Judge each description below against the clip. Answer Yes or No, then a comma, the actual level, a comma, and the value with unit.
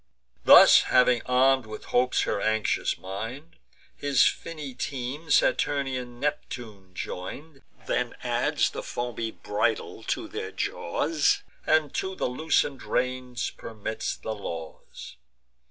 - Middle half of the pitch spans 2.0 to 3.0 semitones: No, average, 4.3 semitones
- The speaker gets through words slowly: Yes, slow, 115 wpm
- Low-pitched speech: Yes, low, 125 Hz